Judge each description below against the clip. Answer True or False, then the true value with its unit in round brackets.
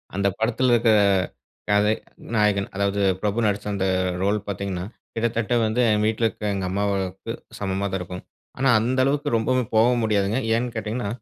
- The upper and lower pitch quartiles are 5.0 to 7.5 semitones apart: False (2.8 semitones)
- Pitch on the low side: True (105 Hz)